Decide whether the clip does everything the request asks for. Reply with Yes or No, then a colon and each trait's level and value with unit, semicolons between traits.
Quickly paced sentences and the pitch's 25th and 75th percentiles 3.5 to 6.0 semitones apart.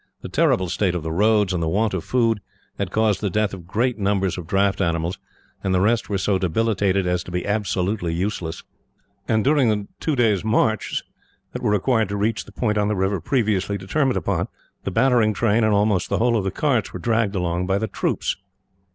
No: fast, 210 wpm; average, 3.1 semitones